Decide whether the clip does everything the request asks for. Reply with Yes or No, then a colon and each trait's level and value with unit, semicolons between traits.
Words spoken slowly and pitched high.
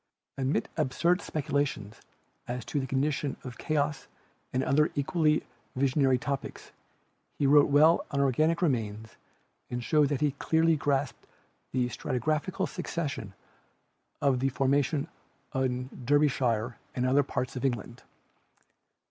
No: slow, 120 wpm; medium, 140 Hz